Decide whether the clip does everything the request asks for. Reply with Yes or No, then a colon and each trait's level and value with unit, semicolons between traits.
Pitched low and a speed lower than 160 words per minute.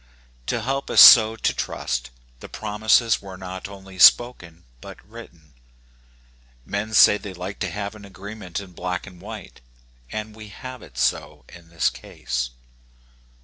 Yes: low, 100 Hz; average, 150 wpm